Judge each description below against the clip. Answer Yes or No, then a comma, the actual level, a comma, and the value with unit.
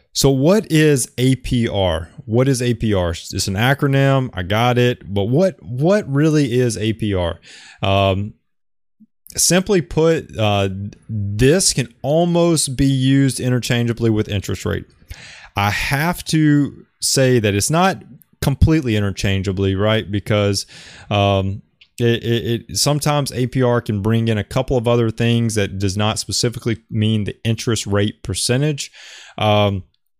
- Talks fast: No, slow, 135 wpm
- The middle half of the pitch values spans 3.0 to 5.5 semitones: Yes, average, 5.1 semitones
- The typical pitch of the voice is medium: No, low, 115 Hz